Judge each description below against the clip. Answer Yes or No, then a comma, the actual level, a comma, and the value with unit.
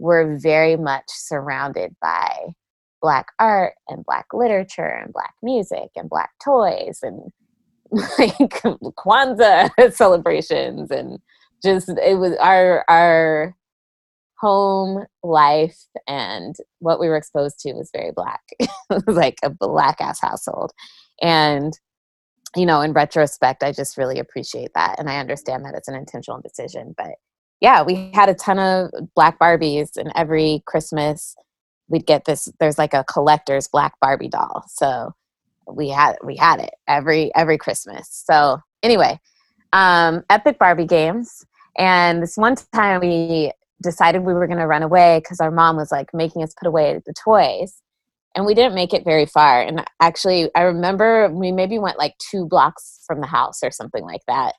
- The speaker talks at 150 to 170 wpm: Yes, average, 160 wpm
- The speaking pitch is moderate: Yes, medium, 170 Hz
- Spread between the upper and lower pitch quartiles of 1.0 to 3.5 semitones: No, average, 4.0 semitones